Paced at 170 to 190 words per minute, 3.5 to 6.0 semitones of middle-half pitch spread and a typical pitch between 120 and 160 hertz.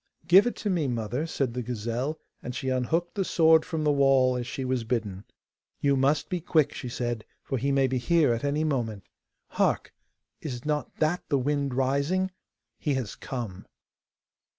Yes: average, 180 wpm; average, 3.9 semitones; low, 135 Hz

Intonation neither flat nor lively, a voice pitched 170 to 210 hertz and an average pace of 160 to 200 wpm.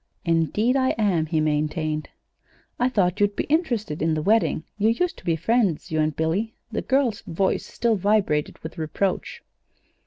No: wide, 6.0 semitones; high, 190 Hz; average, 165 wpm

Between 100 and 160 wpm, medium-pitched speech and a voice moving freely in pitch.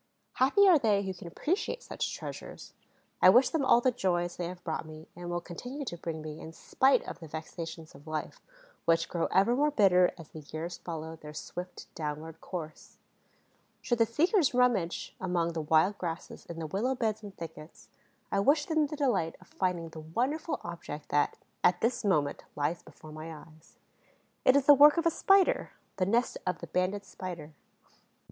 No: average, 190 wpm; medium, 180 Hz; wide, 7.3 semitones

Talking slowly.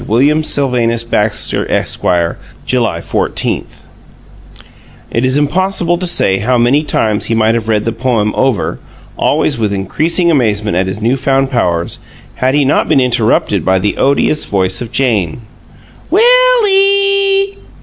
No: average, 145 wpm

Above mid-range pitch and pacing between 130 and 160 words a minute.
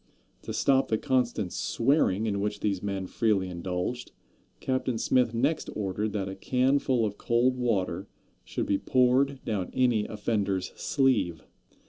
No: low, 110 Hz; average, 140 wpm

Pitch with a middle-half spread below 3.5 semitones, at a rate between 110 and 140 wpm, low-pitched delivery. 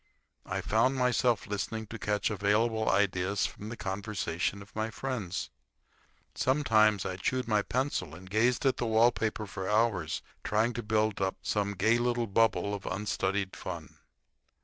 No: average, 2.7 semitones; average, 155 wpm; low, 105 Hz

